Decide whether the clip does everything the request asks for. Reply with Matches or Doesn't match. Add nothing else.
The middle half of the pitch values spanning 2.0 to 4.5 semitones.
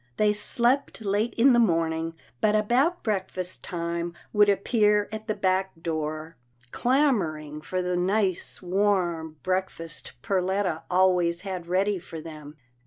Matches